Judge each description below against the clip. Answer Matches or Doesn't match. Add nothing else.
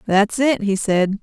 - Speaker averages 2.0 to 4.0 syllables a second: Matches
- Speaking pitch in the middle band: Doesn't match